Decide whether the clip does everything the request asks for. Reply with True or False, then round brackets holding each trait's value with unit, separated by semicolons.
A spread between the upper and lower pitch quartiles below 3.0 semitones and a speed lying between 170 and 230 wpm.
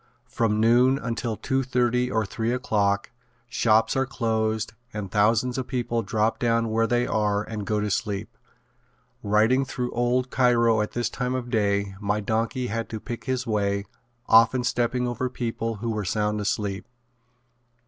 False (2.5 semitones; 160 wpm)